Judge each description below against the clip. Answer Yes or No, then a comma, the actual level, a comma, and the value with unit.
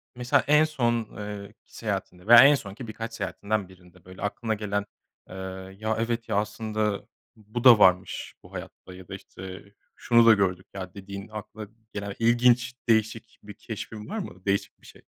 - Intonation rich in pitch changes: No, average, 2.8 semitones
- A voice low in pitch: Yes, low, 105 Hz